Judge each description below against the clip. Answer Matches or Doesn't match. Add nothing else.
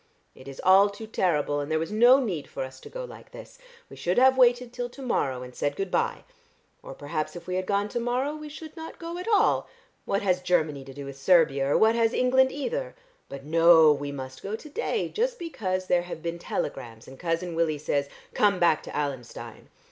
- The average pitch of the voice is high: Doesn't match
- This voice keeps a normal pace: Doesn't match